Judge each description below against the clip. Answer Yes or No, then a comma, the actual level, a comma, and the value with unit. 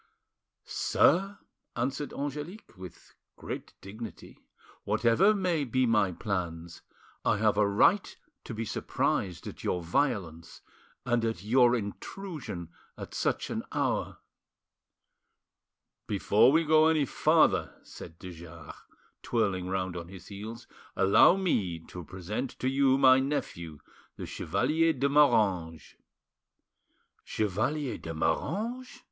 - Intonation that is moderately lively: No, wide, 7.5 semitones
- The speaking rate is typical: No, slow, 115 wpm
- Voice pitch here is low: Yes, low, 115 Hz